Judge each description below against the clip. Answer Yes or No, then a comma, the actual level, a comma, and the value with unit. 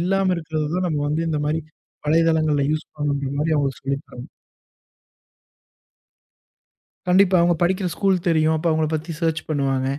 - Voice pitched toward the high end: No, medium, 155 Hz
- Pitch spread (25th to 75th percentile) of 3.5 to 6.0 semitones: No, average, 2.7 semitones